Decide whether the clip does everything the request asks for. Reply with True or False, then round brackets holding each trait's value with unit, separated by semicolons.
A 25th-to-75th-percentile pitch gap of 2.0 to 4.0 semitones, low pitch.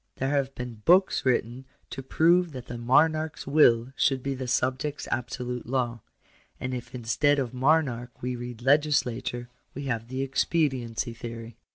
True (2.6 semitones; 130 Hz)